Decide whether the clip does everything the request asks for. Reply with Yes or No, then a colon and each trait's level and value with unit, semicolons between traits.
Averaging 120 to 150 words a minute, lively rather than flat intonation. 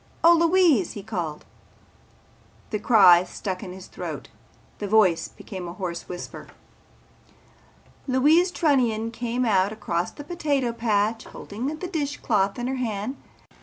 Yes: slow, 135 wpm; wide, 6.3 semitones